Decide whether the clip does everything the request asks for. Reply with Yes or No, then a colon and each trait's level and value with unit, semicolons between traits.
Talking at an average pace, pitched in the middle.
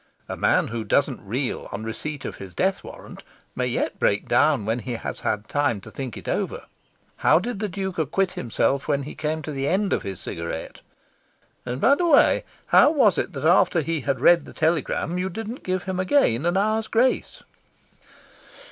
Yes: average, 195 wpm; medium, 155 Hz